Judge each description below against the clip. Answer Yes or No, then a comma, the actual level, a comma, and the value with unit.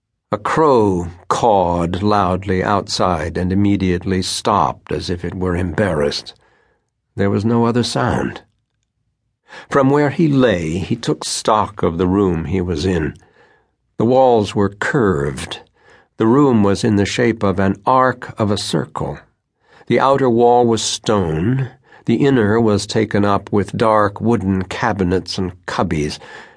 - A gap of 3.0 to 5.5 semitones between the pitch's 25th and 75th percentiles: Yes, average, 4.0 semitones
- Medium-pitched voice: No, low, 105 Hz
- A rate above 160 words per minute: No, average, 140 wpm